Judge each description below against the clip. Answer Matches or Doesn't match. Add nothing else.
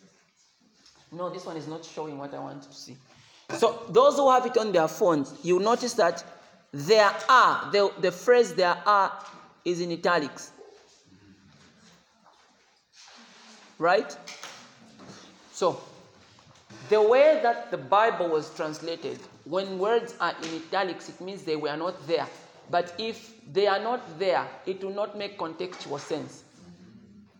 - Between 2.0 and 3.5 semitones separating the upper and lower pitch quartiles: Doesn't match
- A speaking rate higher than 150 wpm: Doesn't match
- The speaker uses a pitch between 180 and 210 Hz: Matches